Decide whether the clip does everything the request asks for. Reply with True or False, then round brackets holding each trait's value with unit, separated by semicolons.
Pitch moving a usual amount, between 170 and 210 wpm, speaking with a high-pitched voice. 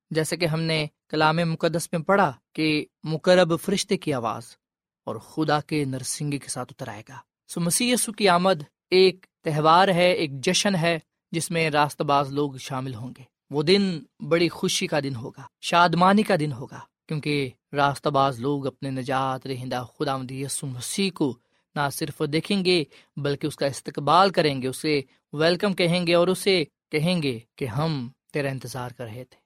False (4.2 semitones; 180 wpm; 155 Hz)